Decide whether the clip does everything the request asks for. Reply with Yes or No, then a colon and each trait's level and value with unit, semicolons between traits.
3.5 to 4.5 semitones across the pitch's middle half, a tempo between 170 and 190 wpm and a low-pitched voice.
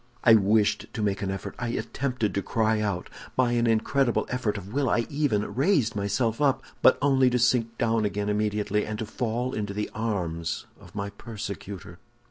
No: average, 2.9 semitones; average, 185 wpm; low, 110 Hz